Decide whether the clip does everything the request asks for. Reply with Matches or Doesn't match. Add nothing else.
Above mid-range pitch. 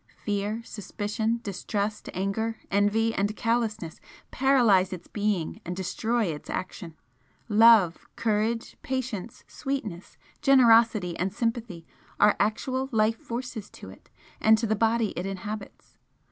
Matches